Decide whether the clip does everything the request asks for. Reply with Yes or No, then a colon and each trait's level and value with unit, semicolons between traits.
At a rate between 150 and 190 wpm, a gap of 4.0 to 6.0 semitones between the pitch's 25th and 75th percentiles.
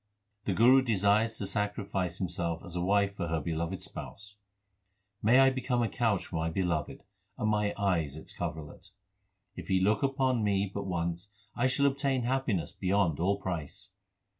Yes: average, 170 wpm; average, 4.5 semitones